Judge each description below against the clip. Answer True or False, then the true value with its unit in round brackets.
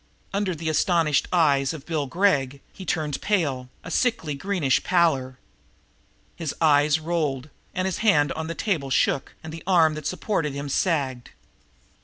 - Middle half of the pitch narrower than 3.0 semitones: False (3.7 semitones)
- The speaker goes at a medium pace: True (155 wpm)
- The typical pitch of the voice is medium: True (155 Hz)